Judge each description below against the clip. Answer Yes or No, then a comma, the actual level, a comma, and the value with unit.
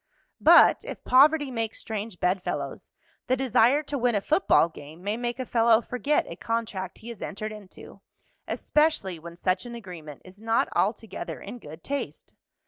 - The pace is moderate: Yes, average, 165 wpm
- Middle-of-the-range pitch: No, high, 225 Hz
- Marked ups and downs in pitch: No, average, 4.9 semitones